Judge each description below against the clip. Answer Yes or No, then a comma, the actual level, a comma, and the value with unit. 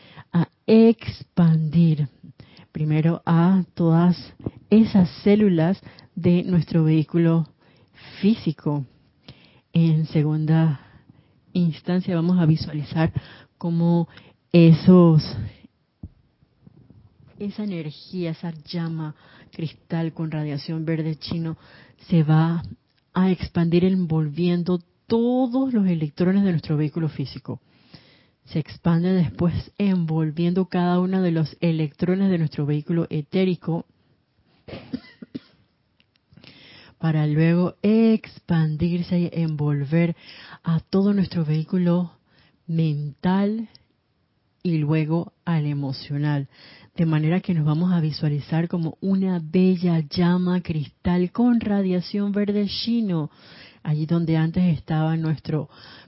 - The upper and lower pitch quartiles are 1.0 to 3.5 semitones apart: Yes, average, 2.8 semitones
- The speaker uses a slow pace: Yes, slow, 95 wpm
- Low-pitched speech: No, medium, 165 Hz